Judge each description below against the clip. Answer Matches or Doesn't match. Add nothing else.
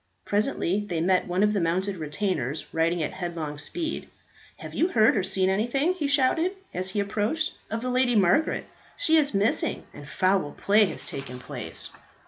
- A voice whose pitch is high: Matches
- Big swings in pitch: Matches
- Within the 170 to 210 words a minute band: Matches